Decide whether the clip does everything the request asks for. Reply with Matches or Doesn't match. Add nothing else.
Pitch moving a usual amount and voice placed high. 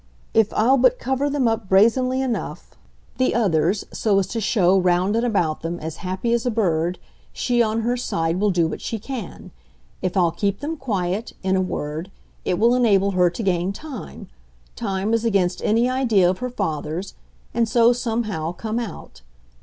Matches